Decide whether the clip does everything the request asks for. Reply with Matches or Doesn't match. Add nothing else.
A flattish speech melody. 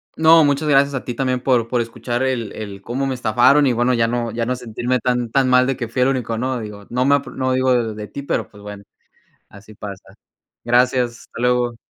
Matches